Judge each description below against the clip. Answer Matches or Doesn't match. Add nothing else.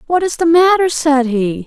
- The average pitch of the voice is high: Matches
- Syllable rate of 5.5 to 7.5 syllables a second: Doesn't match